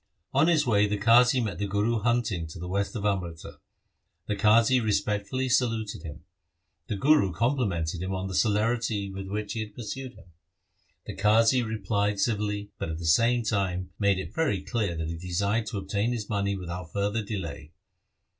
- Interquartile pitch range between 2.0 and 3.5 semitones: Yes, average, 3.2 semitones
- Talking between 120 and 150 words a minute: No, average, 180 wpm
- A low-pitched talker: Yes, low, 105 Hz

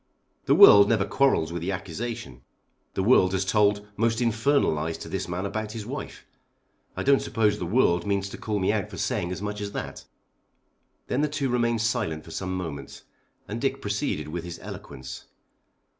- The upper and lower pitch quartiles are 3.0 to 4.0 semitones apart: No, average, 4.4 semitones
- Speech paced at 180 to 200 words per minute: Yes, average, 190 wpm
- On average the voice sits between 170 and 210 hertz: No, low, 105 Hz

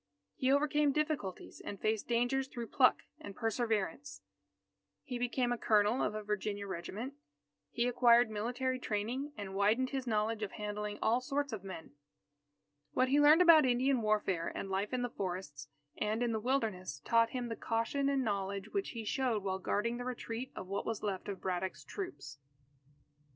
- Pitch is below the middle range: No, high, 225 Hz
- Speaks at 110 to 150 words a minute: No, average, 170 wpm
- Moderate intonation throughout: Yes, average, 4.1 semitones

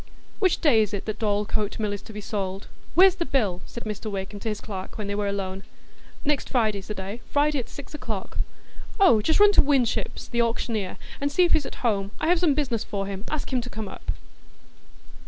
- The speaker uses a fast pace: Yes, fast, 220 wpm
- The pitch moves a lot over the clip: Yes, wide, 5.8 semitones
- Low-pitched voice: No, high, 220 Hz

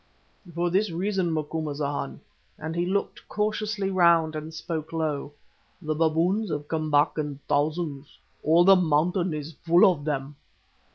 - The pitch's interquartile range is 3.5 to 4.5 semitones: No, average, 2.9 semitones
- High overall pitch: No, medium, 160 Hz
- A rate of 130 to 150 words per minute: Yes, average, 145 wpm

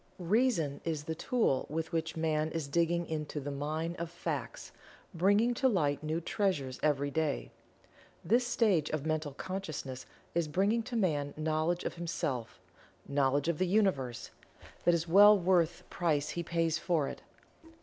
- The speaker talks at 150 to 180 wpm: Yes, average, 160 wpm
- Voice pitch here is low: No, medium, 165 Hz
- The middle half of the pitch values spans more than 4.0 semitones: No, average, 3.7 semitones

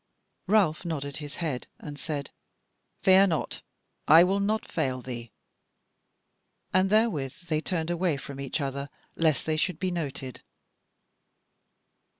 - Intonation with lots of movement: No, average, 4.5 semitones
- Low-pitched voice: No, medium, 160 Hz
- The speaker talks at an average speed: No, slow, 130 wpm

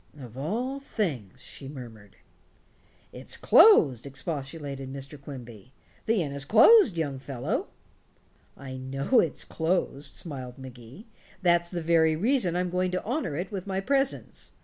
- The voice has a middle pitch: Yes, medium, 150 Hz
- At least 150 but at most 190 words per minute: No, average, 140 wpm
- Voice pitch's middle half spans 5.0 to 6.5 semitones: Yes, wide, 5.6 semitones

